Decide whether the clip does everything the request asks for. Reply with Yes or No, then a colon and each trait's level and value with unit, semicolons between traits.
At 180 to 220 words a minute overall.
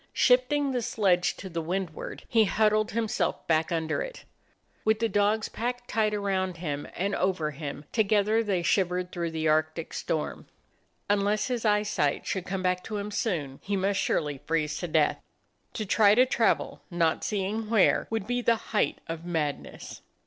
No: average, 165 wpm